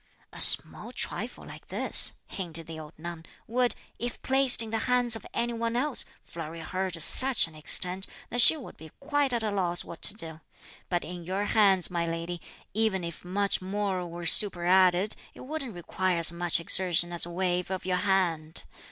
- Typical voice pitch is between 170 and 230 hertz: Yes, medium, 185 Hz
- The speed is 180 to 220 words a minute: Yes, average, 190 wpm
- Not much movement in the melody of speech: No, average, 4.5 semitones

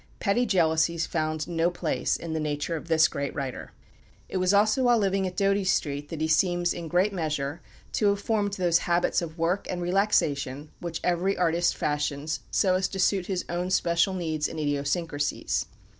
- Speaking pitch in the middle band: Yes, medium, 170 Hz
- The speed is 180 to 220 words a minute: Yes, average, 185 wpm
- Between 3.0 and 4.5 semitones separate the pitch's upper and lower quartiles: Yes, average, 3.3 semitones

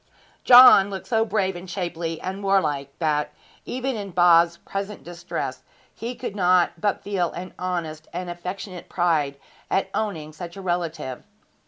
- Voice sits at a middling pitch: Yes, medium, 180 Hz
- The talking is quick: No, average, 150 wpm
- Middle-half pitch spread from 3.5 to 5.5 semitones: No, average, 2.8 semitones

